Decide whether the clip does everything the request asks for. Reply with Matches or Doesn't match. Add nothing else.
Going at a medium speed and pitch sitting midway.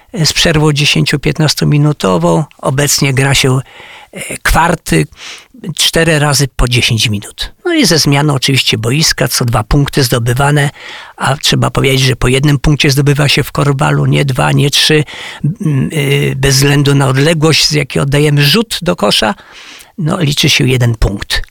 Matches